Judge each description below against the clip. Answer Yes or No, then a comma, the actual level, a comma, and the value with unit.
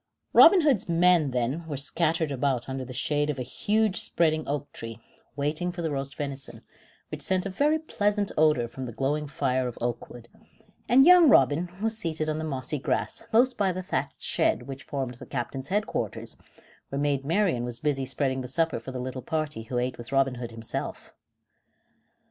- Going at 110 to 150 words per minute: No, average, 190 wpm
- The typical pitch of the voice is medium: Yes, medium, 145 Hz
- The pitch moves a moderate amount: Yes, average, 5.0 semitones